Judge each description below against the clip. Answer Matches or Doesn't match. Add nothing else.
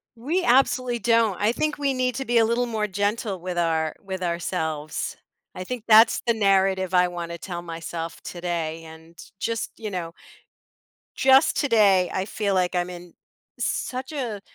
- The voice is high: Matches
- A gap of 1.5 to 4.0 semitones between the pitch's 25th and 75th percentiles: Doesn't match